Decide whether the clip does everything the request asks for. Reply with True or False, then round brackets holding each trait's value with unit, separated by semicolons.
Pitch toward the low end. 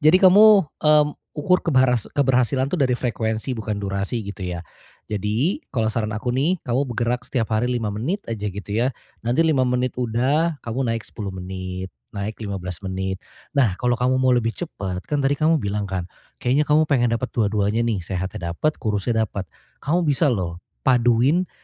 True (120 Hz)